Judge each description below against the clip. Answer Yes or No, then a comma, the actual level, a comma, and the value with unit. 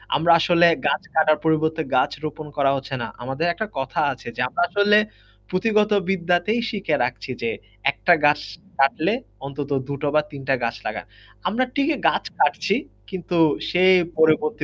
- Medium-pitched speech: Yes, medium, 160 Hz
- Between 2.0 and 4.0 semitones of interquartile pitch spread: No, average, 4.9 semitones